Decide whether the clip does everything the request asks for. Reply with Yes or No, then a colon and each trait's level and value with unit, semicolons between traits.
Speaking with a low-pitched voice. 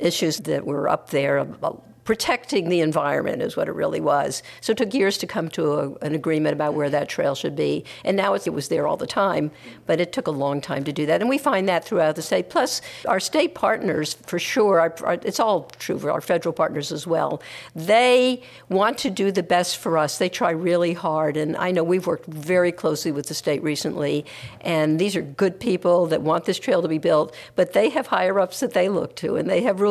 No: medium, 165 Hz